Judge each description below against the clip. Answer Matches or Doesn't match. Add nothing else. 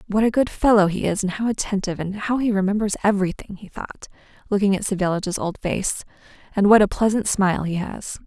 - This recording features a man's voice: Doesn't match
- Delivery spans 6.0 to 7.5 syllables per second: Matches